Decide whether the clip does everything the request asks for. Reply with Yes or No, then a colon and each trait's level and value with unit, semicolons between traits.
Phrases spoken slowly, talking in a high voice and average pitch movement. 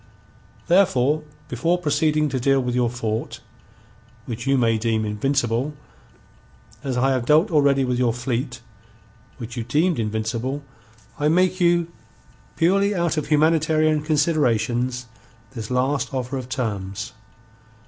No: slow, 130 wpm; low, 135 Hz; average, 4.3 semitones